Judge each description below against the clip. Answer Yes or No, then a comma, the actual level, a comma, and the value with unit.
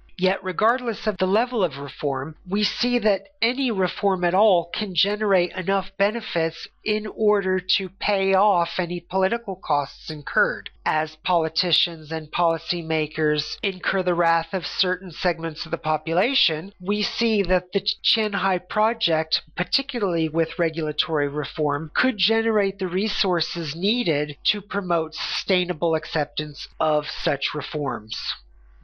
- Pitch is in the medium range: Yes, medium, 180 Hz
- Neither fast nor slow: No, slow, 130 wpm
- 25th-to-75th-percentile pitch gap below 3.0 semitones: No, average, 4.0 semitones